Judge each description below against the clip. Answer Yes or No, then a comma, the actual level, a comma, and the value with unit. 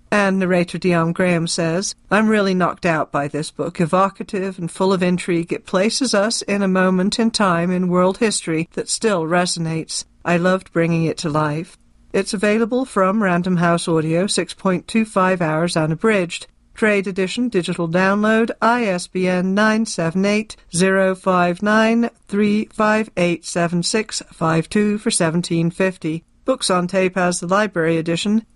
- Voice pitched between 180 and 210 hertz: Yes, medium, 185 Hz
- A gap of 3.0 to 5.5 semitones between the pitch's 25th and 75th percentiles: Yes, average, 3.5 semitones